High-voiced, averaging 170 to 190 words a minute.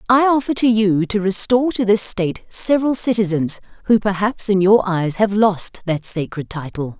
Yes: high, 205 Hz; average, 180 wpm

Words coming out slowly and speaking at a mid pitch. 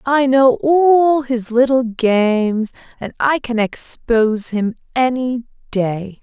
No: slow, 125 wpm; high, 245 Hz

